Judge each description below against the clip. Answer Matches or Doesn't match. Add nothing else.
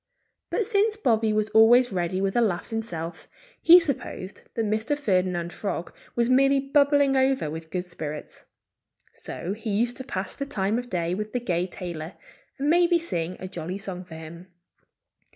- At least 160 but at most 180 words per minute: Matches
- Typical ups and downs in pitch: Doesn't match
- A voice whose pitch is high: Matches